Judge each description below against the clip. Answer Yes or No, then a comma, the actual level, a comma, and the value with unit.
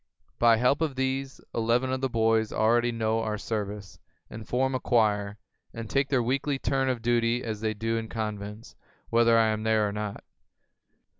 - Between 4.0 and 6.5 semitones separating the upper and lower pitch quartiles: No, narrow, 2.6 semitones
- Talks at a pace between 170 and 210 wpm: Yes, average, 180 wpm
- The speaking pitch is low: Yes, low, 115 Hz